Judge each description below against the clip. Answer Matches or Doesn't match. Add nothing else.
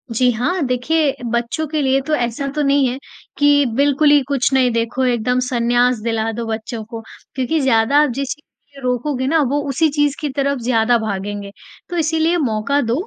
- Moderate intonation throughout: Matches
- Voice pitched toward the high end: Matches